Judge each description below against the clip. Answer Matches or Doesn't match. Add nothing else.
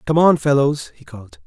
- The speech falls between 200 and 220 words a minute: Matches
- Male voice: Matches